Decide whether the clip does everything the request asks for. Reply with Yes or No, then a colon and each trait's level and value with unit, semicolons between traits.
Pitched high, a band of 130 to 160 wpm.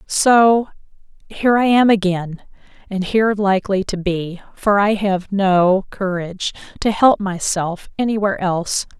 Yes: high, 195 Hz; average, 140 wpm